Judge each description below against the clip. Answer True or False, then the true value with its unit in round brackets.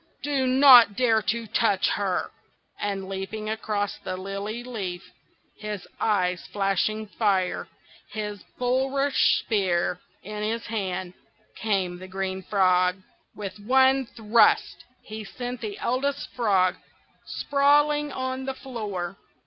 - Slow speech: True (115 wpm)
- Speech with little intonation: False (4.4 semitones)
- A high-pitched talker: True (210 Hz)